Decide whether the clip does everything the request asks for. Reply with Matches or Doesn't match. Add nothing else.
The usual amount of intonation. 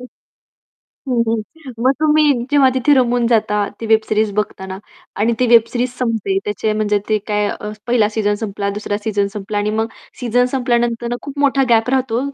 Matches